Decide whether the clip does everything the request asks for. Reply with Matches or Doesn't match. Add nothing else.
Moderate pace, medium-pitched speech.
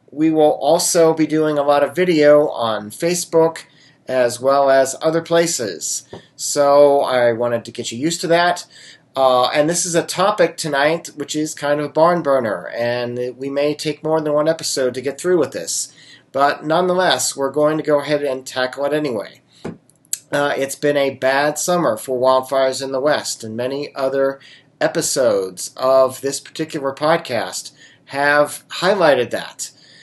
Matches